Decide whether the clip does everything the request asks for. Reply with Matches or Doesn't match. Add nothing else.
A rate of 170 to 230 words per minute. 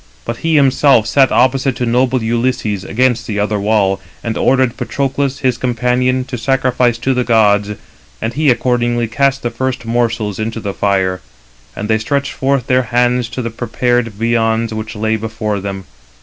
Matches